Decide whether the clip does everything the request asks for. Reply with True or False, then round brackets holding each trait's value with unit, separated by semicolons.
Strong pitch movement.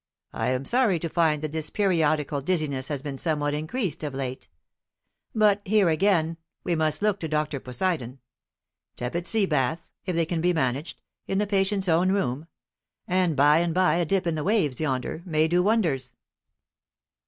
False (4.1 semitones)